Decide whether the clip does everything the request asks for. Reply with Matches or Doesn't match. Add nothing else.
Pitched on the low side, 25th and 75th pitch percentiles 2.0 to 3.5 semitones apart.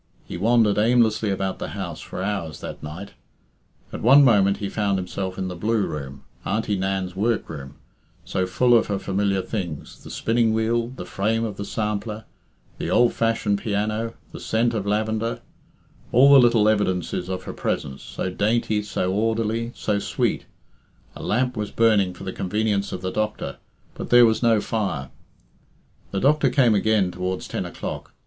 Matches